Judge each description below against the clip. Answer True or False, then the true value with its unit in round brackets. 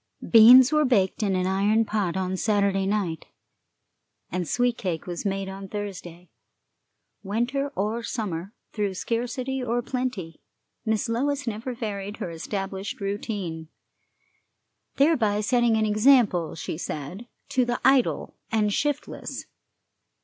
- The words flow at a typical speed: False (125 wpm)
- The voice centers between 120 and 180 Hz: False (210 Hz)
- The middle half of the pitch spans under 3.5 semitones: False (4.1 semitones)